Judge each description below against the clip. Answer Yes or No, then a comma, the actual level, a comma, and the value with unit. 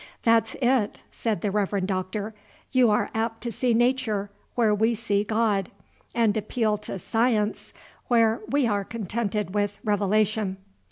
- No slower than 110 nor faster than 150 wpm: Yes, average, 145 wpm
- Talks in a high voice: Yes, high, 215 Hz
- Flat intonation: Yes, narrow, 2.1 semitones